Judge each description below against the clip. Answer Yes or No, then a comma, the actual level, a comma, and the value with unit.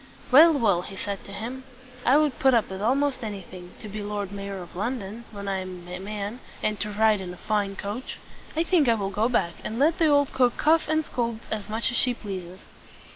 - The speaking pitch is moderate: No, high, 215 Hz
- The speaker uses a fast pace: Yes, fast, 230 wpm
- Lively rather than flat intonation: No, average, 4.4 semitones